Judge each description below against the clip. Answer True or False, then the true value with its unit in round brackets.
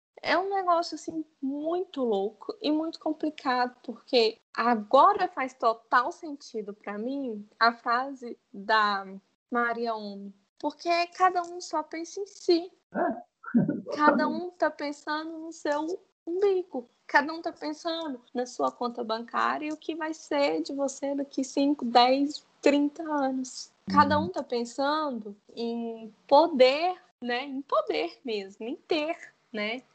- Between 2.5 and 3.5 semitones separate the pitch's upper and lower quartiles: False (5.2 semitones)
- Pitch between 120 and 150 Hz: False (280 Hz)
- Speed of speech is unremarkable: True (135 wpm)